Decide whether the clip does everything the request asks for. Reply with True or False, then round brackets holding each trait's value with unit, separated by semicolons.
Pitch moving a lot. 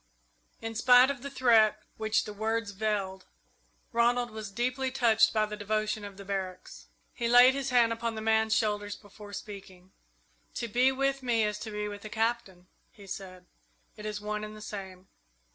False (2.5 semitones)